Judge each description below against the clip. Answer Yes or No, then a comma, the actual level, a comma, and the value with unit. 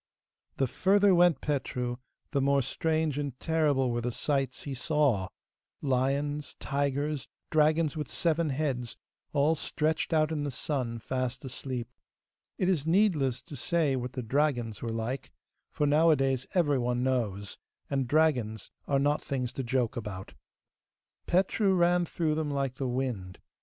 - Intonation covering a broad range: No, average, 3.6 semitones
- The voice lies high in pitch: No, medium, 140 Hz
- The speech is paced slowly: No, average, 145 wpm